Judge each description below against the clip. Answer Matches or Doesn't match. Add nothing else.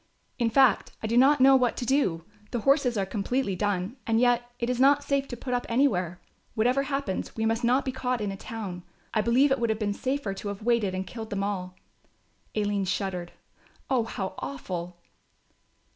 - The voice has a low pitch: Doesn't match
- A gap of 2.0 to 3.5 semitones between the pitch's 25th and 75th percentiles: Doesn't match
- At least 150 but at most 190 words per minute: Doesn't match